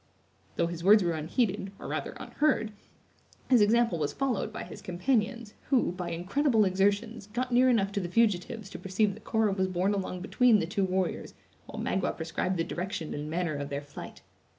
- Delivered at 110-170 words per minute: No, average, 190 wpm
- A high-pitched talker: Yes, high, 195 Hz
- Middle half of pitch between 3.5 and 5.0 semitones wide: Yes, average, 4.2 semitones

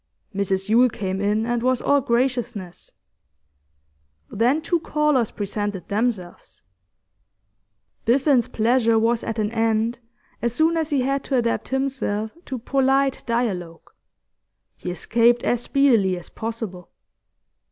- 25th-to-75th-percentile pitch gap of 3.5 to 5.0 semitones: Yes, average, 3.9 semitones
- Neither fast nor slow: No, slow, 120 wpm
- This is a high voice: Yes, high, 235 Hz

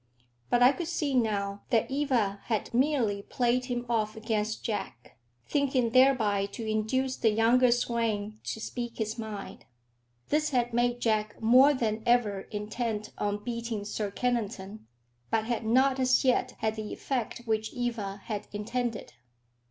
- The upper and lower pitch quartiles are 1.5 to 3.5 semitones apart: Yes, average, 2.7 semitones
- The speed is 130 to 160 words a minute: Yes, average, 150 wpm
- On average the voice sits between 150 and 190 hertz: No, high, 230 Hz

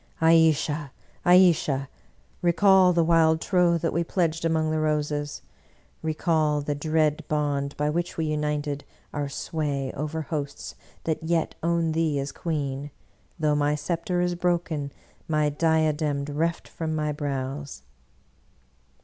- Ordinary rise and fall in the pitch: No, narrow, 2.0 semitones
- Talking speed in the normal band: No, slow, 130 wpm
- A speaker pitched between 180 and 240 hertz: No, medium, 155 Hz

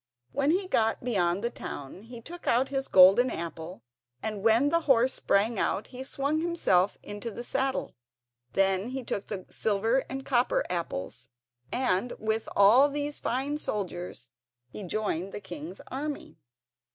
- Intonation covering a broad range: Yes, wide, 5.7 semitones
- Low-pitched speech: No, high, 230 Hz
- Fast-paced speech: No, average, 155 wpm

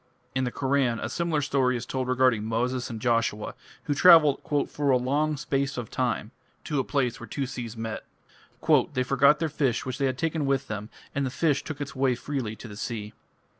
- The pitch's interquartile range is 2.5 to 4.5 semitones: Yes, average, 3.0 semitones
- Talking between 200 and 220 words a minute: Yes, fast, 205 wpm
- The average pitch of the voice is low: Yes, low, 130 Hz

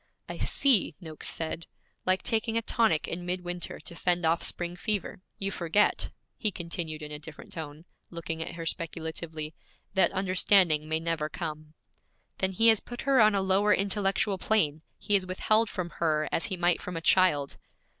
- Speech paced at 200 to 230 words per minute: No, average, 175 wpm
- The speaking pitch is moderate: Yes, medium, 175 Hz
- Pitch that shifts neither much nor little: Yes, average, 3.5 semitones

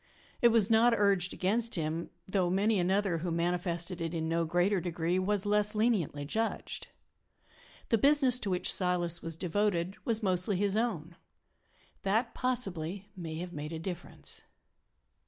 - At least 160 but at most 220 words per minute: No, average, 150 wpm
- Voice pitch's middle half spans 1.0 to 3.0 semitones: No, average, 3.6 semitones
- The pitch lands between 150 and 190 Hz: Yes, medium, 185 Hz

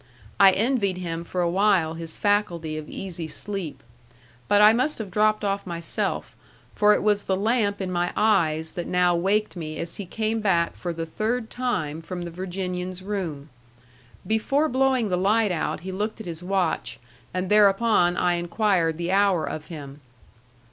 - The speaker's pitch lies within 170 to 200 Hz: Yes, medium, 185 Hz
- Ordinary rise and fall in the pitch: Yes, average, 3.7 semitones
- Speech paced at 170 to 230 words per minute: Yes, average, 175 wpm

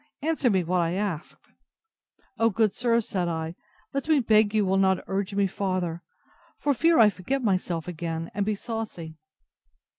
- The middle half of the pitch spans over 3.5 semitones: Yes, average, 4.2 semitones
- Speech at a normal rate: Yes, average, 170 wpm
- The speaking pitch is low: No, high, 195 Hz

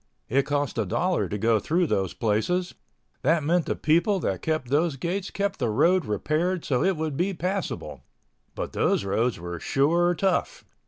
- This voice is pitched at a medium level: Yes, medium, 155 Hz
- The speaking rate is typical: Yes, average, 165 wpm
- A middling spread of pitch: No, wide, 6.5 semitones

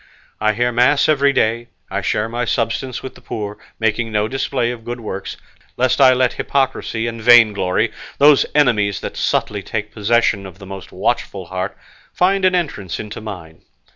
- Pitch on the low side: Yes, low, 115 Hz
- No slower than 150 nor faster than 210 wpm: Yes, average, 170 wpm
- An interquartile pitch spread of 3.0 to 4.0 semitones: Yes, average, 3.7 semitones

